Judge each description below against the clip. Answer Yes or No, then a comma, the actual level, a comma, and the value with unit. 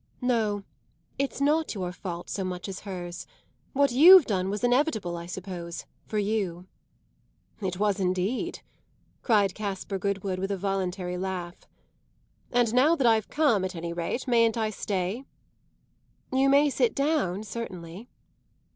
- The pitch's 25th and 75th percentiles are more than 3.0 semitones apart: Yes, average, 5.0 semitones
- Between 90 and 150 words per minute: Yes, average, 140 wpm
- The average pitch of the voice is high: Yes, high, 200 Hz